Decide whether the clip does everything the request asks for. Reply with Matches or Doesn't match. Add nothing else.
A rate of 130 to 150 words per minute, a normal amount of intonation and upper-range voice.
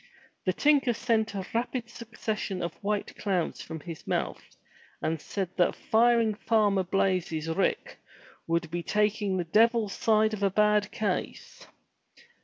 Matches